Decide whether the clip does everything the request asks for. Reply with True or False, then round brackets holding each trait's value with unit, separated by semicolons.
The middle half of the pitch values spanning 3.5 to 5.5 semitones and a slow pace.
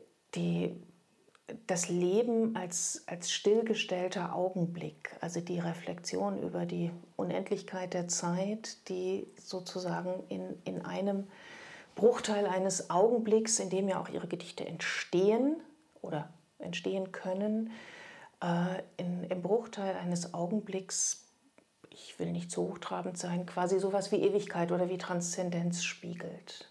False (2.8 semitones; 120 wpm)